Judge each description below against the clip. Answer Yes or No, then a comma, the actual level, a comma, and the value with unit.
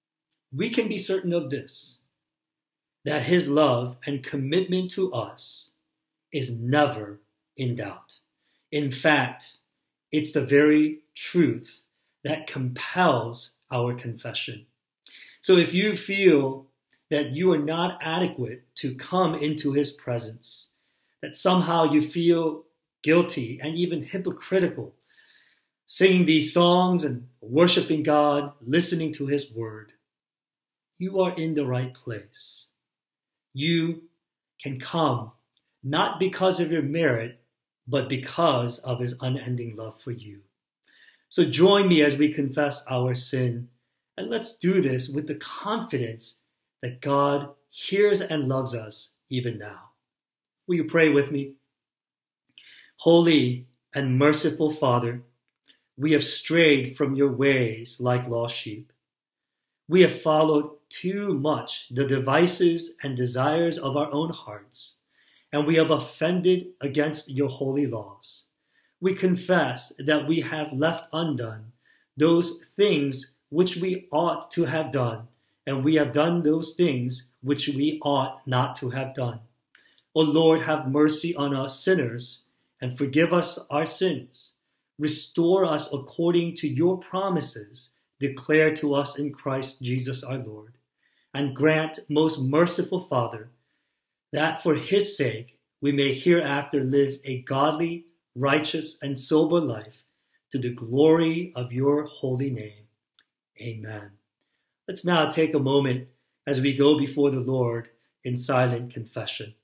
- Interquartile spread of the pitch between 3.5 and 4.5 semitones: Yes, average, 4.2 semitones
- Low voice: No, medium, 145 Hz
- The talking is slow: Yes, slow, 130 wpm